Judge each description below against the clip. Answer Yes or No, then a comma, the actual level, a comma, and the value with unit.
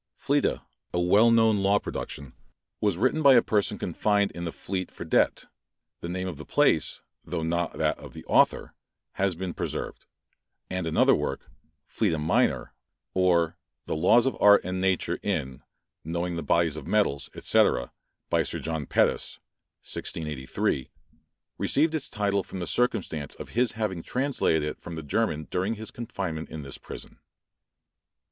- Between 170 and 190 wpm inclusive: No, average, 160 wpm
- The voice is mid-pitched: No, very low, 90 Hz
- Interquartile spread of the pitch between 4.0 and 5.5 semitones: Yes, average, 4.6 semitones